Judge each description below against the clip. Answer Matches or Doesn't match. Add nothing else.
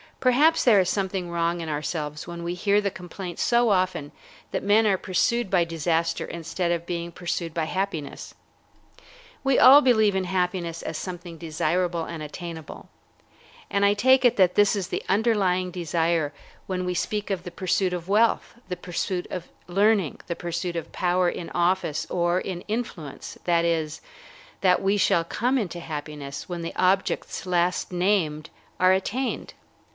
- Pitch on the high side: Doesn't match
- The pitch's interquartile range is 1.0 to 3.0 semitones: Matches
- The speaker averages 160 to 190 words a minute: Matches